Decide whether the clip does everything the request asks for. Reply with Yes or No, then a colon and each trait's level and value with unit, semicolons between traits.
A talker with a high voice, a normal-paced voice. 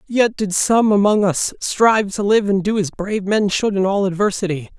No: high, 200 Hz; fast, 215 wpm